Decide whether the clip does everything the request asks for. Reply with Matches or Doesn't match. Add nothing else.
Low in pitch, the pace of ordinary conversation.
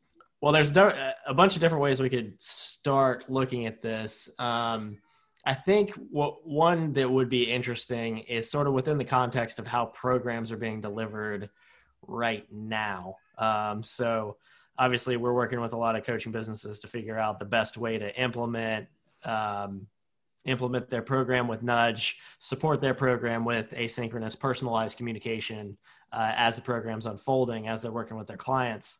Matches